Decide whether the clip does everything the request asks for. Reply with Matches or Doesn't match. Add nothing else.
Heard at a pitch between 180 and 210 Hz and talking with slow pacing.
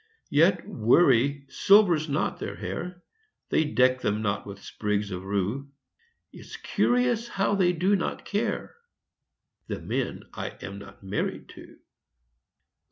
Doesn't match